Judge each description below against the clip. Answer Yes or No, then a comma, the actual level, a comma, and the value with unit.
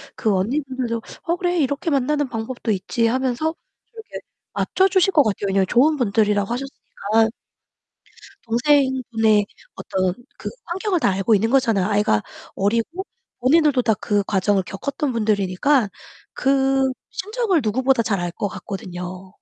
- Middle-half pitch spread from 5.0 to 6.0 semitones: Yes, wide, 5.6 semitones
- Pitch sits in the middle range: No, high, 235 Hz